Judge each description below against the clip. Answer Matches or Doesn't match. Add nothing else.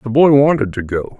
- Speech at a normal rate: Doesn't match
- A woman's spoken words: Doesn't match